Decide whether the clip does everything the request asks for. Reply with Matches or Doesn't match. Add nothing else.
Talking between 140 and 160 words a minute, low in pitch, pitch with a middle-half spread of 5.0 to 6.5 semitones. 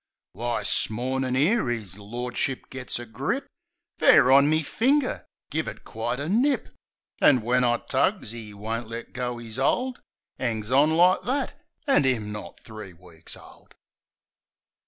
Matches